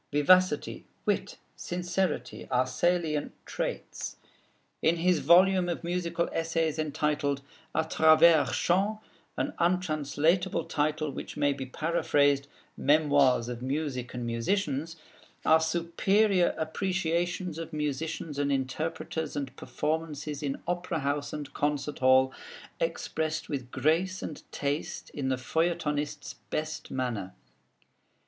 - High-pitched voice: No, medium, 155 Hz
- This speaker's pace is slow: Yes, slow, 110 wpm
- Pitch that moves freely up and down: No, average, 3.2 semitones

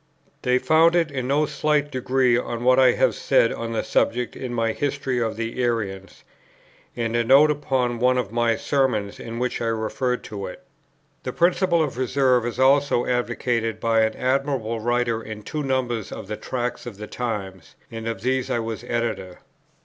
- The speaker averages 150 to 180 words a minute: No, average, 190 wpm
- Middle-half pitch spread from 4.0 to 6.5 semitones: No, narrow, 2.5 semitones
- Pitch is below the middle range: Yes, low, 120 Hz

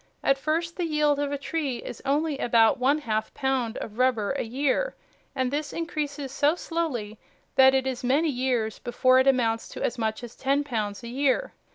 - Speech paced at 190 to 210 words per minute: Yes, average, 195 wpm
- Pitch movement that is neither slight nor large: Yes, average, 3.4 semitones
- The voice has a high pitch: Yes, very high, 265 Hz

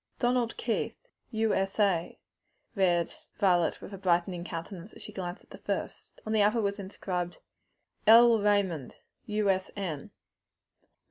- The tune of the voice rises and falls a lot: No, average, 3.2 semitones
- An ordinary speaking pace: No, slow, 125 wpm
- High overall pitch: Yes, high, 195 Hz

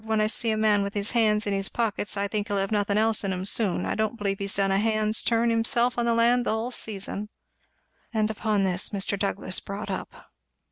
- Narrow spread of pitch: Yes, narrow, 2.0 semitones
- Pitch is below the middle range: No, high, 210 Hz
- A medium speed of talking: No, fast, 235 wpm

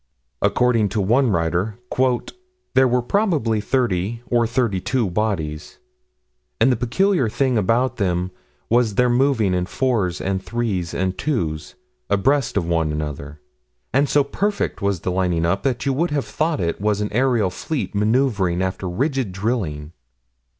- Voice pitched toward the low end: Yes, low, 110 Hz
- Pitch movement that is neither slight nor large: No, wide, 5.8 semitones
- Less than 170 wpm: Yes, average, 150 wpm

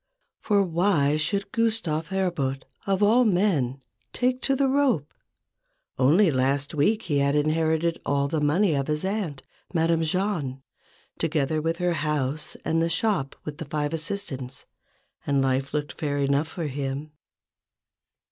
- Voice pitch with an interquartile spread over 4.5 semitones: Yes, average, 5.2 semitones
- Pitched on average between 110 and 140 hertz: No, medium, 155 Hz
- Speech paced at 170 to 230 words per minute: No, average, 145 wpm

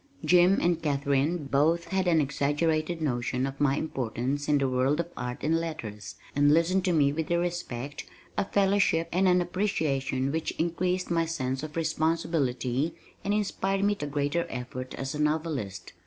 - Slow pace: No, average, 170 wpm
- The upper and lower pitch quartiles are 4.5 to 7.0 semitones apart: No, average, 4.0 semitones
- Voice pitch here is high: No, medium, 155 Hz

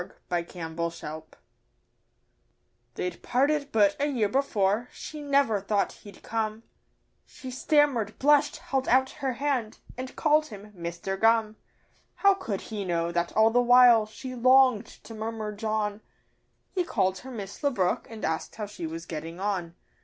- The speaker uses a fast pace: No, average, 160 wpm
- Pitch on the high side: Yes, high, 220 Hz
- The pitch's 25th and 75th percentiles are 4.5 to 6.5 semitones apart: Yes, average, 5.1 semitones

